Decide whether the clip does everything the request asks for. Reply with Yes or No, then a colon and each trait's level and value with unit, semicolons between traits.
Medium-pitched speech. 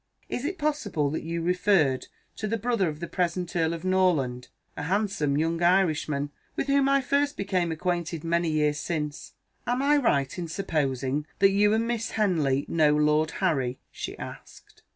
Yes: medium, 170 Hz